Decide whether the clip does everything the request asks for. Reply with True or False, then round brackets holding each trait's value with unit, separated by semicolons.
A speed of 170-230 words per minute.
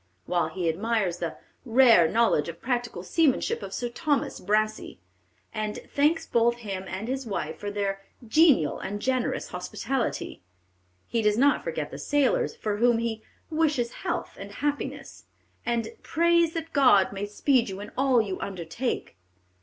False (155 wpm)